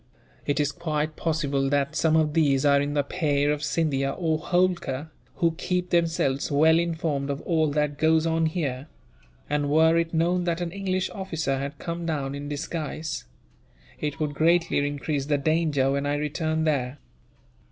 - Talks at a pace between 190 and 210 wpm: No, average, 170 wpm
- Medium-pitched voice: Yes, medium, 155 Hz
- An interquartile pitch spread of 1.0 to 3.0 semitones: Yes, narrow, 2.5 semitones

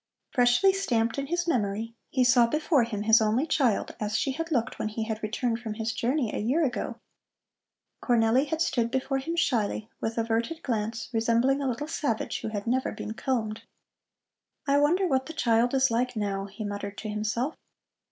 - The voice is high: Yes, high, 235 Hz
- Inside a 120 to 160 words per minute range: No, average, 185 wpm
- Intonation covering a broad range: No, average, 3.6 semitones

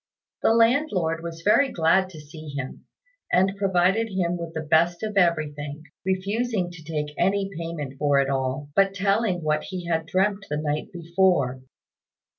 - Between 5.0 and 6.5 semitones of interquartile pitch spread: No, average, 4.2 semitones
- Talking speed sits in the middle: Yes, average, 160 wpm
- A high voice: No, medium, 170 Hz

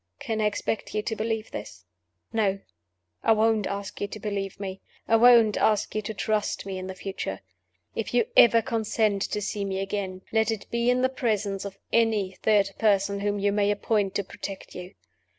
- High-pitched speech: Yes, high, 210 Hz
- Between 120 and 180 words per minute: No, average, 195 wpm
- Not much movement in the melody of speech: Yes, narrow, 2.1 semitones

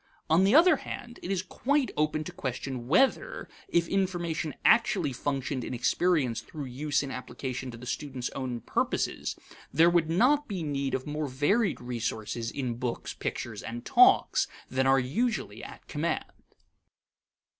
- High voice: No, medium, 145 Hz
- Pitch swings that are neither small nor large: No, wide, 6.5 semitones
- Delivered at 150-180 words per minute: Yes, average, 155 wpm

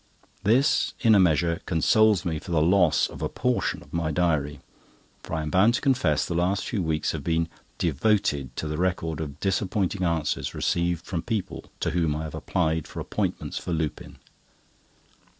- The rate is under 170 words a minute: No, average, 180 wpm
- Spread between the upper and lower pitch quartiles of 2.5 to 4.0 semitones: Yes, average, 3.5 semitones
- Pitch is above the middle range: No, very low, 85 Hz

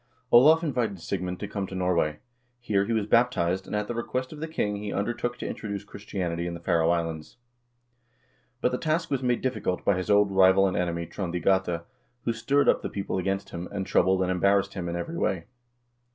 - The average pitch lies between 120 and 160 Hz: No, low, 100 Hz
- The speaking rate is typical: No, fast, 215 wpm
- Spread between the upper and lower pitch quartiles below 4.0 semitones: No, average, 4.6 semitones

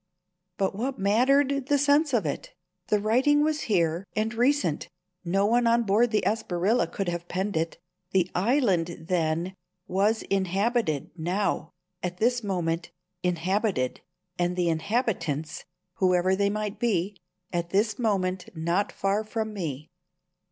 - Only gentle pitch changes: No, average, 4.7 semitones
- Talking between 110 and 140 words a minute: Yes, slow, 135 wpm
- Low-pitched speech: No, high, 195 Hz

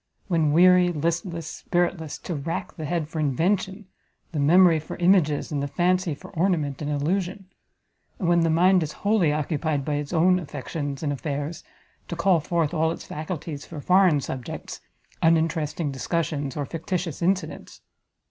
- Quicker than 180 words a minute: No, average, 155 wpm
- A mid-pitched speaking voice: Yes, medium, 165 Hz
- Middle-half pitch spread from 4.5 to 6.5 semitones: No, average, 3.1 semitones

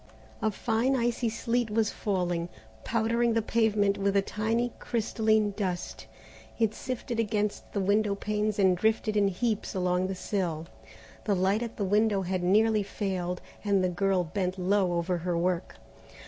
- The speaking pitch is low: No, high, 205 Hz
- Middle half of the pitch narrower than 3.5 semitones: Yes, average, 3.1 semitones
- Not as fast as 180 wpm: Yes, average, 160 wpm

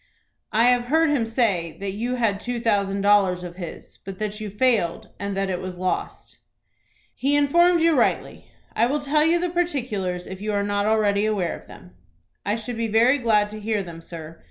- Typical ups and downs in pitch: Yes, average, 4.2 semitones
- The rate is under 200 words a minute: No, fast, 205 wpm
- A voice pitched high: Yes, high, 215 Hz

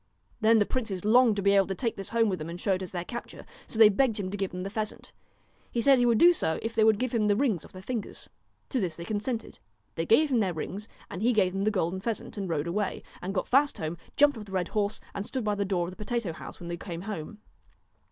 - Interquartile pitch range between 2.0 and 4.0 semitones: Yes, average, 3.7 semitones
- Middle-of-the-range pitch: No, high, 205 Hz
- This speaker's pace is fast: Yes, fast, 280 wpm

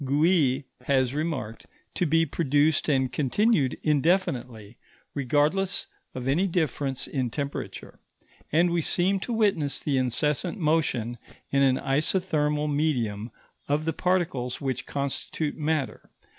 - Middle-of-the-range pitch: Yes, medium, 145 Hz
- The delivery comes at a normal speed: No, slow, 120 wpm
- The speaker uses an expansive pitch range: No, average, 3.8 semitones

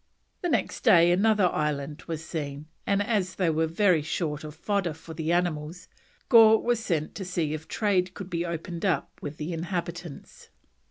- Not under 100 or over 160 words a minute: No, average, 175 wpm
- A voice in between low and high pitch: Yes, medium, 170 Hz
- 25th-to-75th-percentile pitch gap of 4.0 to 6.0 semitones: No, average, 3.5 semitones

